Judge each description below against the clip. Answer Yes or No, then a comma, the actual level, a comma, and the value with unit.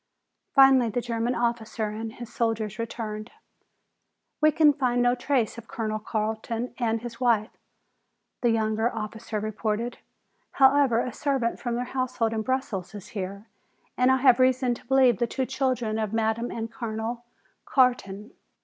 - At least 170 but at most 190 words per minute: No, average, 150 wpm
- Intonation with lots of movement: No, narrow, 2.4 semitones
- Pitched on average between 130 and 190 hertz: No, high, 235 Hz